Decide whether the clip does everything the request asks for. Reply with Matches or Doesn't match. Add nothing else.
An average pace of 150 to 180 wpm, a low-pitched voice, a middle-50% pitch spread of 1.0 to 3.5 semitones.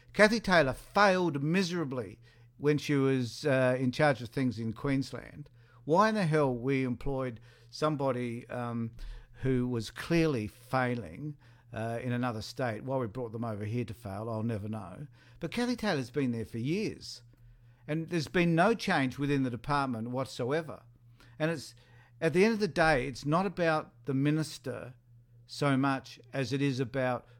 Doesn't match